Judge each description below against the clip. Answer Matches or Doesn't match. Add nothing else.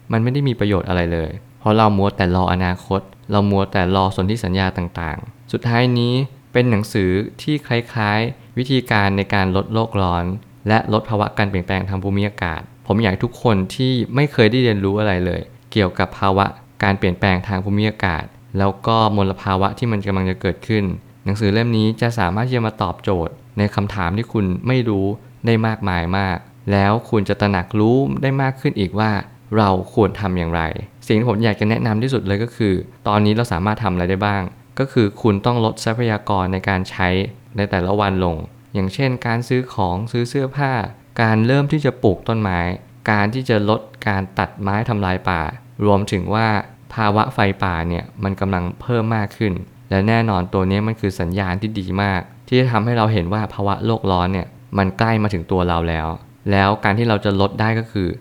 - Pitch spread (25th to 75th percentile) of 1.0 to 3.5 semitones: Matches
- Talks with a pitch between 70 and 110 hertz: Matches